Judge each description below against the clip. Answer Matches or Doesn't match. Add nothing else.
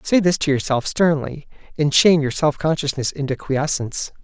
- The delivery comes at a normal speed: Matches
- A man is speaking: Matches